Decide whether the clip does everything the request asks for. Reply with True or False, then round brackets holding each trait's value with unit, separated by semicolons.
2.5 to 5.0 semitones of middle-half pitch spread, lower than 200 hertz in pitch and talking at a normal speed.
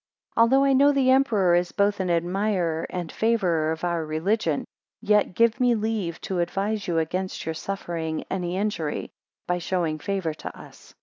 True (4.3 semitones; 185 Hz; 170 wpm)